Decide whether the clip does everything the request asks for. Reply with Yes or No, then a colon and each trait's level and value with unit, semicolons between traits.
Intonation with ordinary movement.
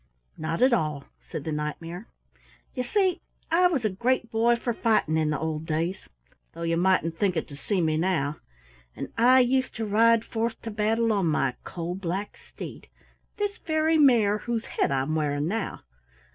No: wide, 6.6 semitones